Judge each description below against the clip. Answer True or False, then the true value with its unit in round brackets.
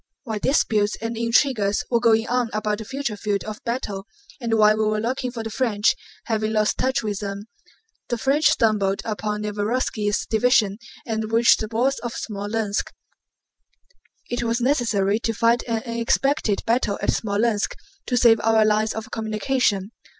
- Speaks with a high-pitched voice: True (220 Hz)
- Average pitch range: False (2.2 semitones)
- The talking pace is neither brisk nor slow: True (155 wpm)